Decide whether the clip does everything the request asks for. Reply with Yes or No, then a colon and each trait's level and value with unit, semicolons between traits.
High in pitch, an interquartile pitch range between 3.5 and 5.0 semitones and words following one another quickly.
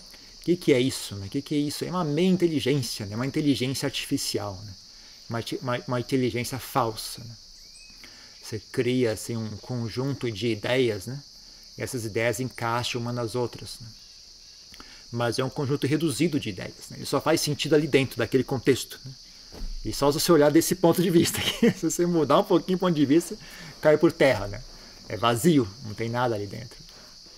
No: low, 130 Hz; average, 4.5 semitones; fast, 195 wpm